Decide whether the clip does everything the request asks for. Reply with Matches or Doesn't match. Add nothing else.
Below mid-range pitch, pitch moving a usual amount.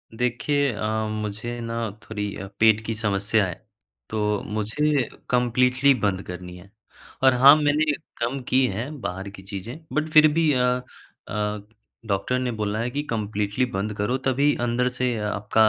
Matches